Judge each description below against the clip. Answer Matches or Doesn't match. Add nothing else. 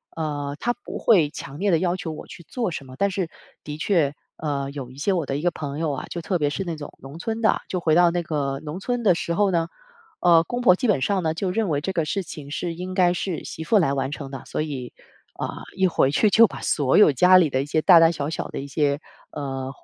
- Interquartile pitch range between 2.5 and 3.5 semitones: Doesn't match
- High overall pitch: Doesn't match